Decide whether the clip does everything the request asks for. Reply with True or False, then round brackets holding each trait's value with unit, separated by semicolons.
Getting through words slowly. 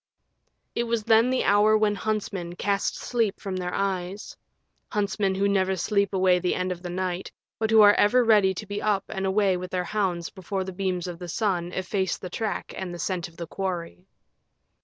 False (200 wpm)